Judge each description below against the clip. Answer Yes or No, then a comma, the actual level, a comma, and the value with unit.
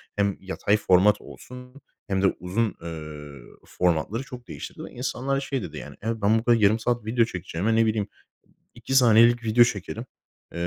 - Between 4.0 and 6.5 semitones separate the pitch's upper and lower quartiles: Yes, average, 4.5 semitones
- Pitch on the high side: No, low, 110 Hz